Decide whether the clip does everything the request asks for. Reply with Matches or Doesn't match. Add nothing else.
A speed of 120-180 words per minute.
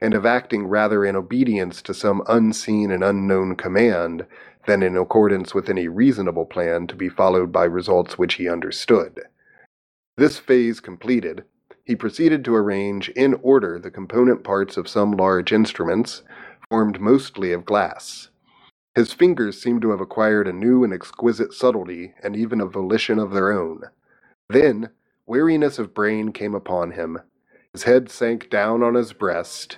Matches